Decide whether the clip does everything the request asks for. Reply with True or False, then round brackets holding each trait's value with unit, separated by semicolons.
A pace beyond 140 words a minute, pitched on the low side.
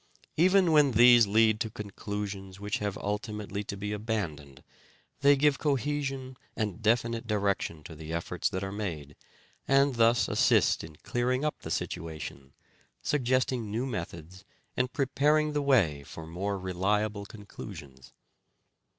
False (135 wpm; 105 Hz)